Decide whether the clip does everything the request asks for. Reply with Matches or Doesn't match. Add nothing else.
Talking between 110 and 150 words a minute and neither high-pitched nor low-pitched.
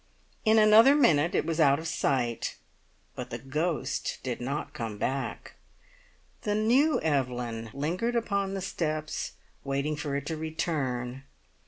Matches